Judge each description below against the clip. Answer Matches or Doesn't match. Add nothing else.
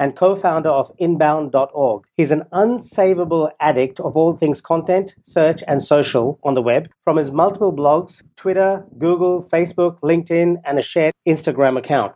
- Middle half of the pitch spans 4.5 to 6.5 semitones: Doesn't match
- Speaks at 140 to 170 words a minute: Matches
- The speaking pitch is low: Doesn't match